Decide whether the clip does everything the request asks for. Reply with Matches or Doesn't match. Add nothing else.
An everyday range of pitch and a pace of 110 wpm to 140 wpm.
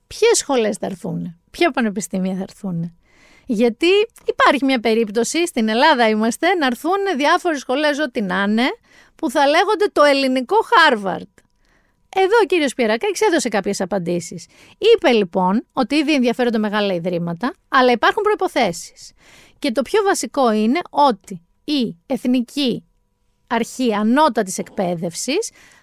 Doesn't match